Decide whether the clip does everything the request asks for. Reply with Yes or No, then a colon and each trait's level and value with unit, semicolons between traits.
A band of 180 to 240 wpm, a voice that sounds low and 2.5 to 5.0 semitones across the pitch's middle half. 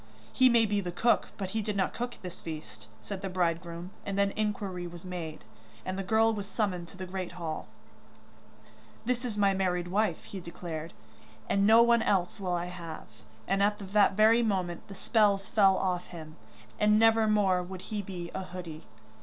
No: average, 190 wpm; high, 190 Hz; average, 3.0 semitones